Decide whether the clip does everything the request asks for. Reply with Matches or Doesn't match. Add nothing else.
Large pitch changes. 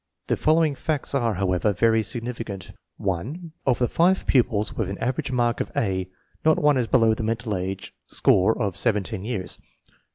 Doesn't match